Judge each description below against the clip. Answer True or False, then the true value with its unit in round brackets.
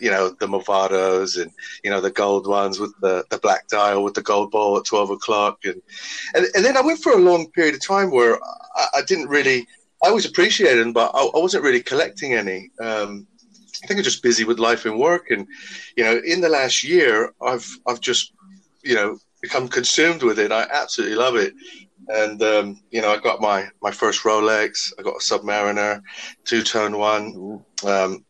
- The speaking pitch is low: True (115 Hz)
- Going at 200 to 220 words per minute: True (205 wpm)